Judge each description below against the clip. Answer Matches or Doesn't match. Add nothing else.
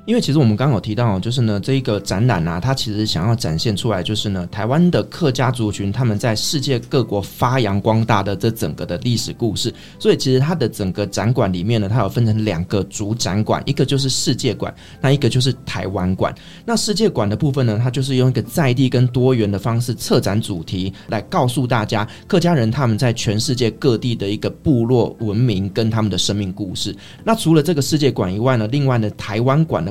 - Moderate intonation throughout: Matches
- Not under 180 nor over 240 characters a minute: Doesn't match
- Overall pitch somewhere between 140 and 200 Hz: Doesn't match